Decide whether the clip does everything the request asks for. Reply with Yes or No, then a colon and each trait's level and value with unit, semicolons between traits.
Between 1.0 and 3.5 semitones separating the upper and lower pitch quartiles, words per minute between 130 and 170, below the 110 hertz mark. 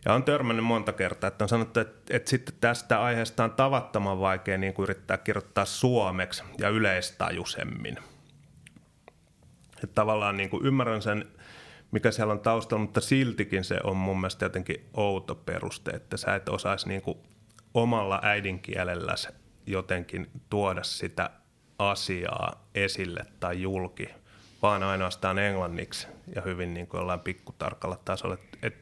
Yes: average, 3.1 semitones; average, 135 wpm; low, 100 Hz